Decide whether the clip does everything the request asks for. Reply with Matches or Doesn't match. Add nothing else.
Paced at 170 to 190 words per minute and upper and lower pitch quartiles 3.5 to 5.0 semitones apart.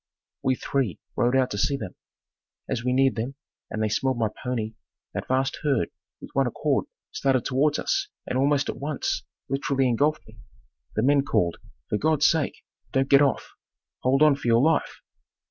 Doesn't match